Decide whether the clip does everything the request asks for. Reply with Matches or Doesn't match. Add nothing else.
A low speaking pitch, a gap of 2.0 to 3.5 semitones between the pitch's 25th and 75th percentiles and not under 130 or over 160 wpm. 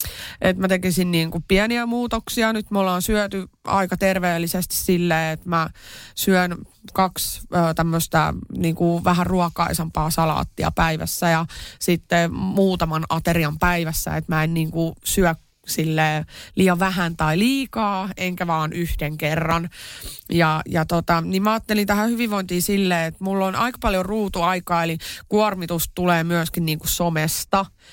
Doesn't match